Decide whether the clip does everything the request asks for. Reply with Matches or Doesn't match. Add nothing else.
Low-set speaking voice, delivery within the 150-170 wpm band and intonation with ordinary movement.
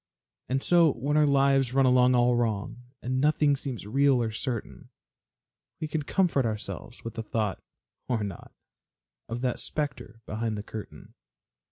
Matches